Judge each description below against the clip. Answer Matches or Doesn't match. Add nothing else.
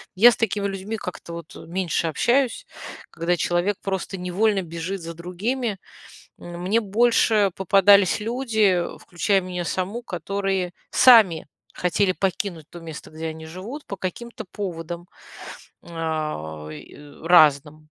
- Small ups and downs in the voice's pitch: Doesn't match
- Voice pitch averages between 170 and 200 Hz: Matches